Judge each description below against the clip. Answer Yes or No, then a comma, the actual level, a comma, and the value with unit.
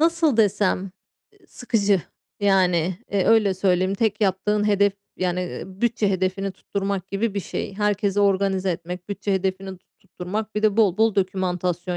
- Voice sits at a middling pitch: No, high, 195 Hz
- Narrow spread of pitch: Yes, narrow, 1.9 semitones